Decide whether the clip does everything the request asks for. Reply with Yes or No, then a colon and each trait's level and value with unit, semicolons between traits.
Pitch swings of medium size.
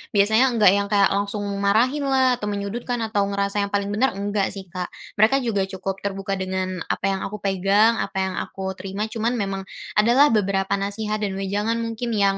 No: narrow, 2.2 semitones